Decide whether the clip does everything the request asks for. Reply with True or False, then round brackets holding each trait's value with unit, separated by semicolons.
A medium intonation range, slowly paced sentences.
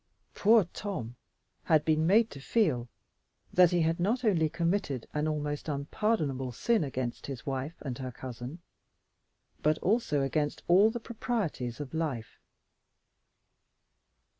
False (6.2 semitones; 130 wpm)